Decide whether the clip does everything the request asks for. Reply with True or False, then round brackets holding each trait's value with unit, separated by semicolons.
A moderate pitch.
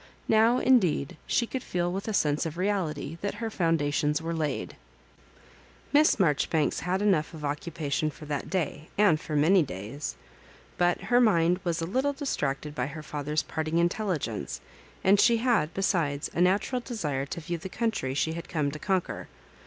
True (170 Hz)